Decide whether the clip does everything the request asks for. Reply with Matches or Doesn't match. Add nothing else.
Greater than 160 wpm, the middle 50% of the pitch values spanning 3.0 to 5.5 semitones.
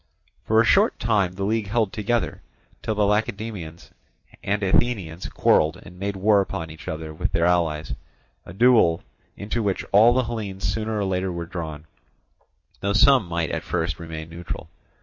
Matches